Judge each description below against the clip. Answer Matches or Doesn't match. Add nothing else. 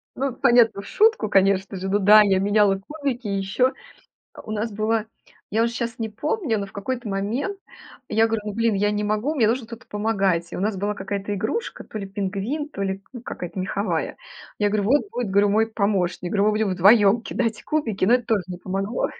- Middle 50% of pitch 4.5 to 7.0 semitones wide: Doesn't match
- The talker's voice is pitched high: Matches